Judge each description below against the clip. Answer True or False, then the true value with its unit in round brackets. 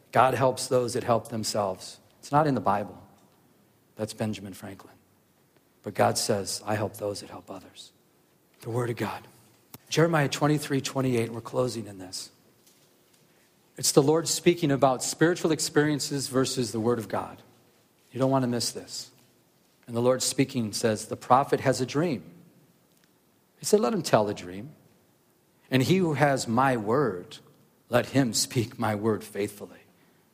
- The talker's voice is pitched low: True (120 Hz)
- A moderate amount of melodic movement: True (4.1 semitones)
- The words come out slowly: False (160 wpm)